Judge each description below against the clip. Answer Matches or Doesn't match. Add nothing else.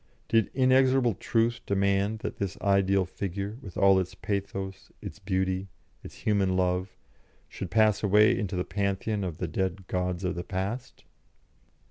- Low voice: Matches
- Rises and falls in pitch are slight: Matches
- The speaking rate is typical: Matches